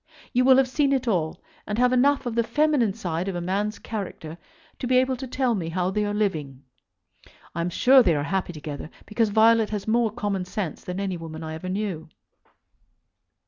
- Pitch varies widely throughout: Yes, wide, 5.7 semitones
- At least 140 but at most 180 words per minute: No, fast, 205 wpm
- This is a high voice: Yes, high, 205 Hz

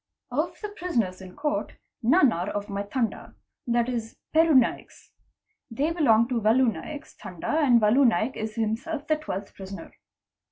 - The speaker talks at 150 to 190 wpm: Yes, average, 160 wpm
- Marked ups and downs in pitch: Yes, wide, 5.7 semitones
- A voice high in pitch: Yes, high, 235 Hz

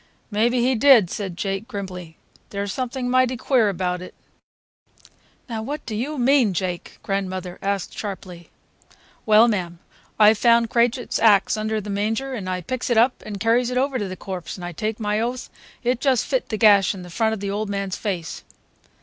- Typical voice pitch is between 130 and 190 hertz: No, high, 215 Hz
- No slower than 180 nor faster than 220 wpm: Yes, average, 190 wpm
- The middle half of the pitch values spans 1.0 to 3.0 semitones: No, average, 3.9 semitones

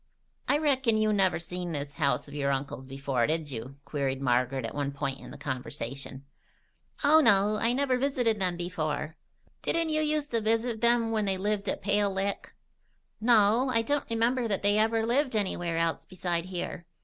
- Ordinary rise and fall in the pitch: No, wide, 8.0 semitones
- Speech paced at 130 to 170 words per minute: No, average, 180 wpm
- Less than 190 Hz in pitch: No, high, 195 Hz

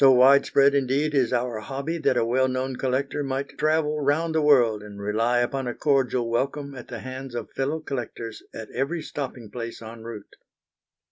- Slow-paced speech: No, average, 185 wpm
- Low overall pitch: Yes, low, 130 Hz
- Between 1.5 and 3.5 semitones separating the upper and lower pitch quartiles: Yes, average, 2.9 semitones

